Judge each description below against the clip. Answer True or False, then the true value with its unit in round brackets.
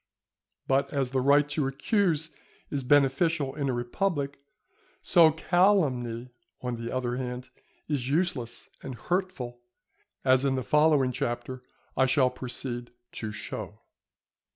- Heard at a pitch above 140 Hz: False (135 Hz)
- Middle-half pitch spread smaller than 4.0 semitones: True (3.4 semitones)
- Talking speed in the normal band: False (130 wpm)